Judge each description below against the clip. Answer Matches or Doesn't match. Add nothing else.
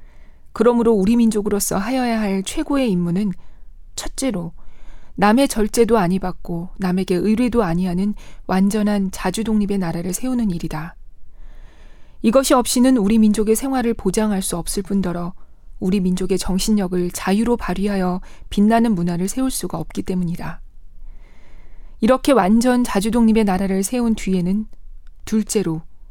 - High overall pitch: Matches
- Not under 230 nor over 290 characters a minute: Doesn't match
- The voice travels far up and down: Doesn't match